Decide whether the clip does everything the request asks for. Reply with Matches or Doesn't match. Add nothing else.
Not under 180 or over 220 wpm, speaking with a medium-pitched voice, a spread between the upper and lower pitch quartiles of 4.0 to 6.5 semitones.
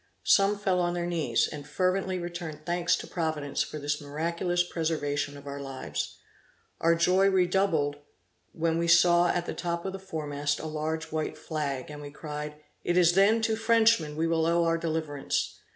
Doesn't match